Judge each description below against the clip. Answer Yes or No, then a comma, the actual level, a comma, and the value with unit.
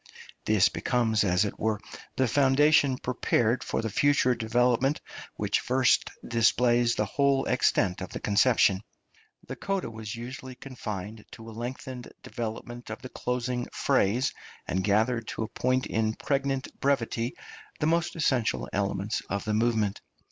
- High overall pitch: No, low, 120 Hz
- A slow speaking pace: No, average, 145 wpm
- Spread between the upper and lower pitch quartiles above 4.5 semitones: No, average, 3.1 semitones